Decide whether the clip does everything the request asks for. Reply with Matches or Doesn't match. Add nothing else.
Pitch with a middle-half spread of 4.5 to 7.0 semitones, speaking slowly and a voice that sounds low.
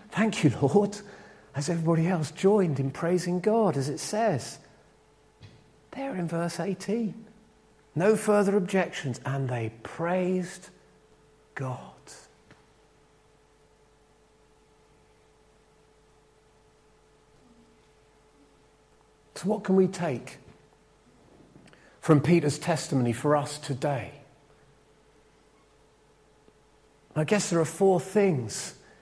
Doesn't match